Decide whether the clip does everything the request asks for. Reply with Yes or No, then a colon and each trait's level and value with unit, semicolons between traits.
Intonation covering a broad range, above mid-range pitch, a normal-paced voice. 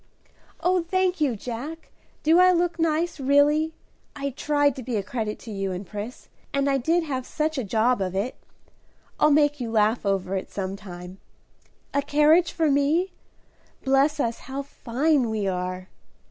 Yes: wide, 6.4 semitones; very high, 275 Hz; average, 170 wpm